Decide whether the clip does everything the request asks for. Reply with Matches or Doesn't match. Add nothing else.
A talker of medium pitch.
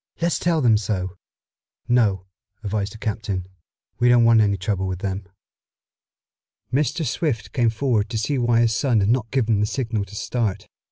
Doesn't match